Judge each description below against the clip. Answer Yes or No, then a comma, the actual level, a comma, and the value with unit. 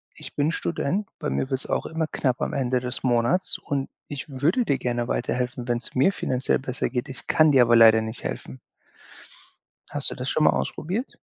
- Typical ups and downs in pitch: Yes, average, 3.4 semitones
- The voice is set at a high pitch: No, low, 130 Hz